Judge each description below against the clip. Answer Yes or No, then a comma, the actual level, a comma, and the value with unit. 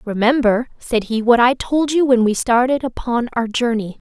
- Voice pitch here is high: Yes, high, 240 Hz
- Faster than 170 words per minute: Yes, average, 190 wpm